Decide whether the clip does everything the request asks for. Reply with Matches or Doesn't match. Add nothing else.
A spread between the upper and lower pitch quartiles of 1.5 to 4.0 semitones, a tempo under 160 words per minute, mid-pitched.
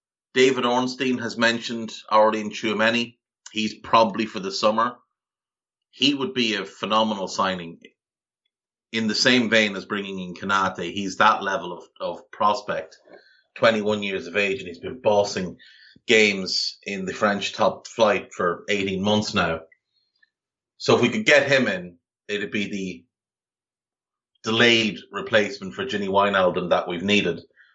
Doesn't match